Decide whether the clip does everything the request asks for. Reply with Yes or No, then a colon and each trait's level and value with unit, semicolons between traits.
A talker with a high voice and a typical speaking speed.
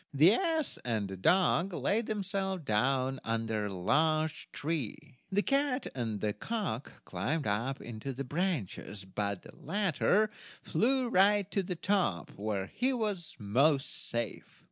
No: medium, 150 Hz; average, 145 wpm